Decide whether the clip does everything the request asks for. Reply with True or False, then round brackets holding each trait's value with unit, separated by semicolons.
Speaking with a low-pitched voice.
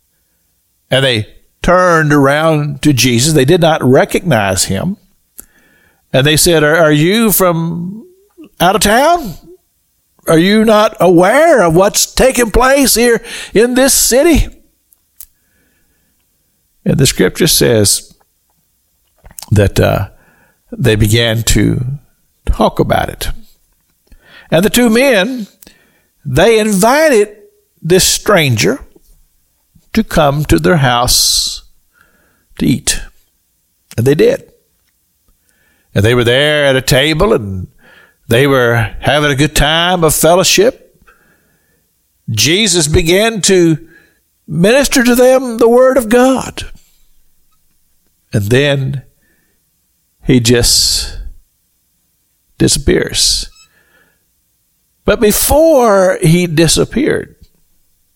False (150 Hz)